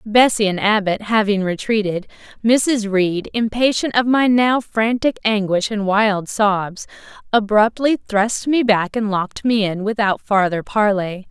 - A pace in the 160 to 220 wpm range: No, average, 145 wpm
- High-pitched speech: Yes, high, 210 Hz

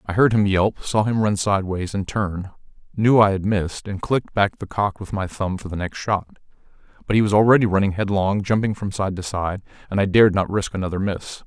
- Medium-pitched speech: No, low, 100 Hz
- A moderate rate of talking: No, fast, 230 wpm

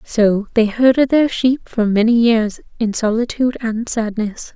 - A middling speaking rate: Yes, average, 160 wpm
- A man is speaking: No, female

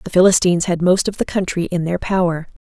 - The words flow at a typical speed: No, fast, 230 wpm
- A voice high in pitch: No, medium, 180 Hz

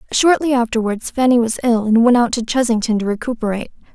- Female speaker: Yes, female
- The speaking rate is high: No, average, 185 wpm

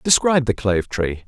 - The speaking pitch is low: Yes, low, 125 Hz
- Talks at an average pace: Yes, average, 190 wpm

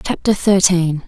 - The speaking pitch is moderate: Yes, medium, 180 Hz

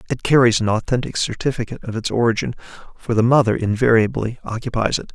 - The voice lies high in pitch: No, low, 115 Hz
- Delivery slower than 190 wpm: Yes, average, 165 wpm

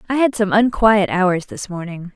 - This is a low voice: No, high, 205 Hz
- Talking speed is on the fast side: No, average, 195 wpm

